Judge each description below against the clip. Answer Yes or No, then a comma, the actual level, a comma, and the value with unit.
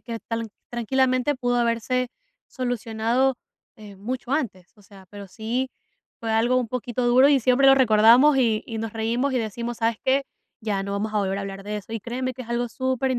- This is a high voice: Yes, high, 235 Hz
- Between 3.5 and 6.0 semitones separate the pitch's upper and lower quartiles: No, average, 2.7 semitones